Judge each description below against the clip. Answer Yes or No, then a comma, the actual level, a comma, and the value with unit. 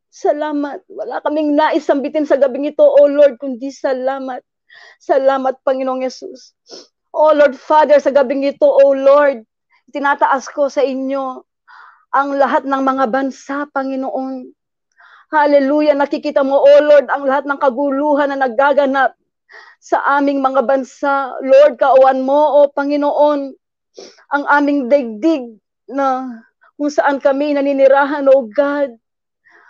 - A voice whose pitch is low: No, very high, 280 Hz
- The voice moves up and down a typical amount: No, narrow, 1.3 semitones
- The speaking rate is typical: No, slow, 125 wpm